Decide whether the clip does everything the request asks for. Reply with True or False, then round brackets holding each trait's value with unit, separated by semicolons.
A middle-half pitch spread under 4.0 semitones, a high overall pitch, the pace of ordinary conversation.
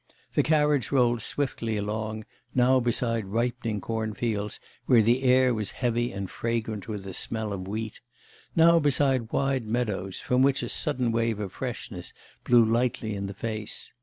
False (2.8 semitones; 115 Hz; 160 wpm)